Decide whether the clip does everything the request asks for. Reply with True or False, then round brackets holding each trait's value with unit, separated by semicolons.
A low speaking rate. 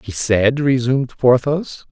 True (125 wpm)